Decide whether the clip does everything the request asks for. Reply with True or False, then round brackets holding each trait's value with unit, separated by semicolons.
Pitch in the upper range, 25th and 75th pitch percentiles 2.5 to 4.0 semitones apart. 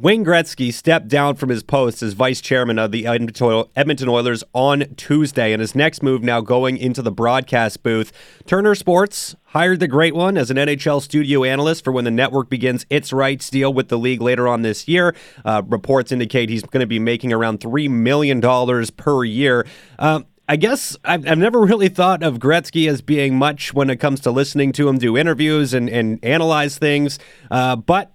False (135 Hz; 3.7 semitones)